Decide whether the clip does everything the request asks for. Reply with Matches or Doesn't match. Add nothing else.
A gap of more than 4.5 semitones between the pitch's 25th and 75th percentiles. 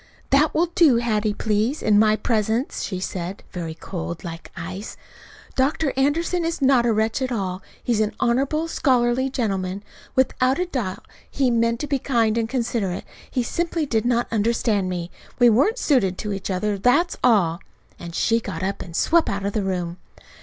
Matches